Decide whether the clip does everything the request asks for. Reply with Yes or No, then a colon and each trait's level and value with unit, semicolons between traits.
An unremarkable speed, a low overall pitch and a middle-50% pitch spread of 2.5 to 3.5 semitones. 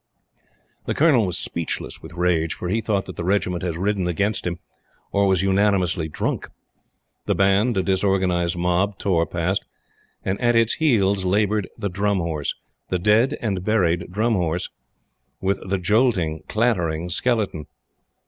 Yes: average, 150 wpm; very low, 95 Hz; average, 3.0 semitones